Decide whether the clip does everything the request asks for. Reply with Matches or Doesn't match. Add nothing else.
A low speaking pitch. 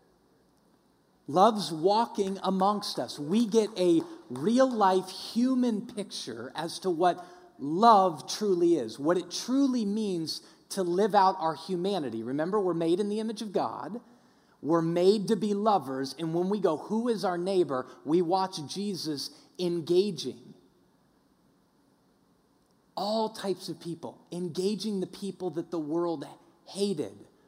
Doesn't match